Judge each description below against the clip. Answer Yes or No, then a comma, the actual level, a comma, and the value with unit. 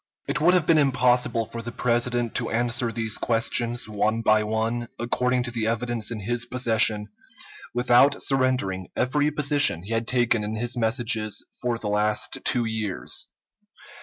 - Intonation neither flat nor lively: No, narrow, 2.1 semitones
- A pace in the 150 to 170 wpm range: Yes, average, 160 wpm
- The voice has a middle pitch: No, low, 120 Hz